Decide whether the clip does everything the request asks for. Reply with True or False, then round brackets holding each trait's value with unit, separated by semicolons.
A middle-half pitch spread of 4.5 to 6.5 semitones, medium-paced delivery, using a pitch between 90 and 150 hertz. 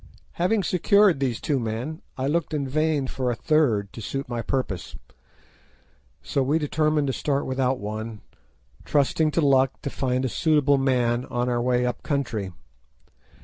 False (3.7 semitones; 160 wpm; 135 Hz)